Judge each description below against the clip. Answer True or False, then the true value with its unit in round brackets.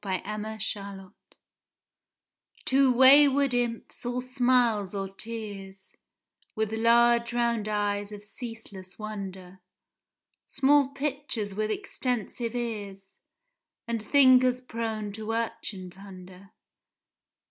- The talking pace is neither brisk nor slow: False (95 wpm)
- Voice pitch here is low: False (220 Hz)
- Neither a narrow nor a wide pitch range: True (3.5 semitones)